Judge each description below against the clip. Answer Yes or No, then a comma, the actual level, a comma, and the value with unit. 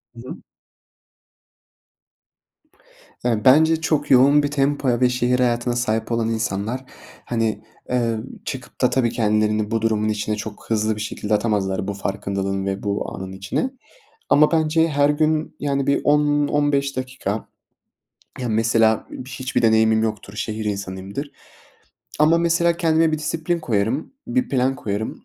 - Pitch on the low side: Yes, low, 120 Hz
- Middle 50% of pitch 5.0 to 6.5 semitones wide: Yes, average, 5.3 semitones